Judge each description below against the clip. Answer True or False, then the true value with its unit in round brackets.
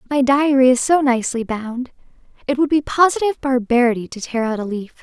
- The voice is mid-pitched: False (260 Hz)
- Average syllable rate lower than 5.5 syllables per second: False (5.9 syllables/s)